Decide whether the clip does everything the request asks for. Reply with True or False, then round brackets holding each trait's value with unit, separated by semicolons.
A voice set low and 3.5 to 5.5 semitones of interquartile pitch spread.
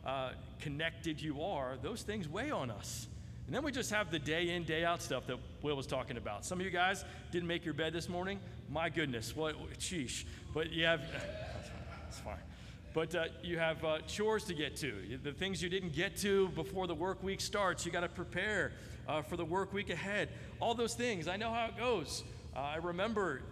False (170 Hz; 4.0 semitones)